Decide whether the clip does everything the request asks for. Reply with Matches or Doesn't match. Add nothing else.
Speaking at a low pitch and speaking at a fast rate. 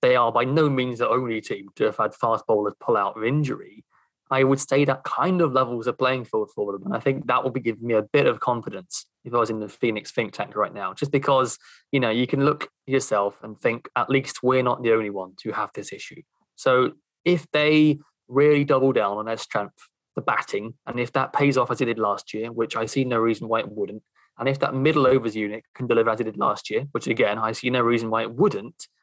Matches